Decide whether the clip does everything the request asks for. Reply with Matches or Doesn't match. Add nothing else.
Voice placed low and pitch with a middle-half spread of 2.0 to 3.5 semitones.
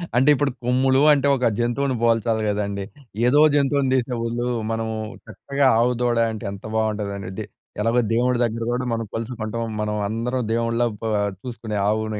Matches